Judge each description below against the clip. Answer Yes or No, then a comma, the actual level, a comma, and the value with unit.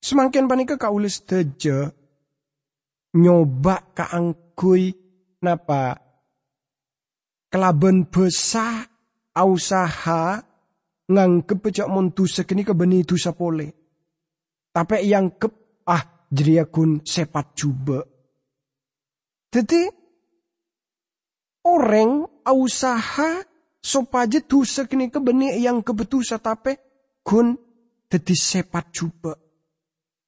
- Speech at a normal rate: No, slow, 85 wpm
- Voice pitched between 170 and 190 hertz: Yes, medium, 185 Hz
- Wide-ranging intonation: Yes, wide, 6.6 semitones